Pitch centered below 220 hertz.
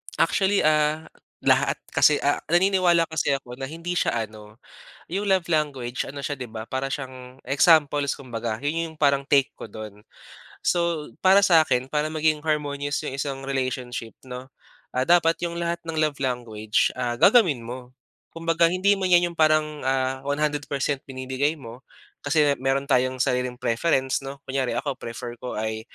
Yes: medium, 140 Hz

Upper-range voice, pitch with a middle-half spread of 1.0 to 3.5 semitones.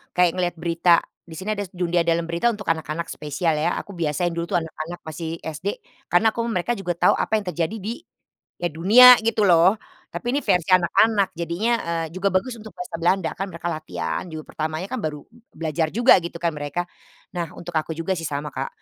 No: medium, 175 Hz; average, 3.2 semitones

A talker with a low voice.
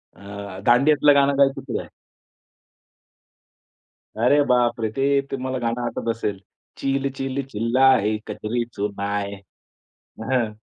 Yes: low, 120 Hz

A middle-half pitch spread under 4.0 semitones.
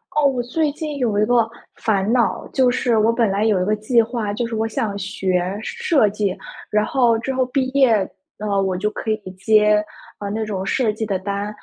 Yes: average, 3.2 semitones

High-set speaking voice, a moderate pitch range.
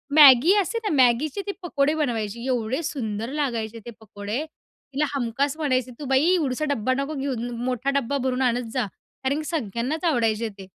Yes: very high, 260 Hz; average, 4.0 semitones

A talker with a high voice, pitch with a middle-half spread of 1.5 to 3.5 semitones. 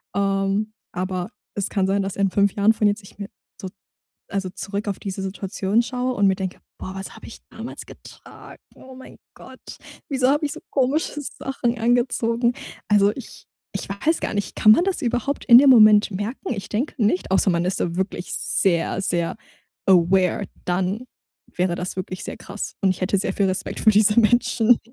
No: high, 200 Hz; average, 3.9 semitones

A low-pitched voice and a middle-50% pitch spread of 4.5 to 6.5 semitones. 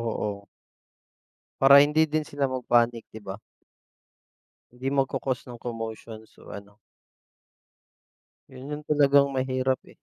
No: low, 130 Hz; average, 3.5 semitones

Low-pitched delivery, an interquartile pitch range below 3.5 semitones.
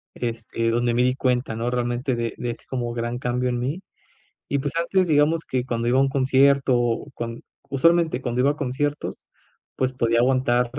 Yes: low, 125 Hz; narrow, 2.4 semitones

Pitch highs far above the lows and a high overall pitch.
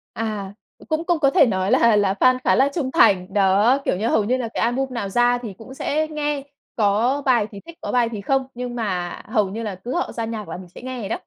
No: average, 4.5 semitones; high, 230 Hz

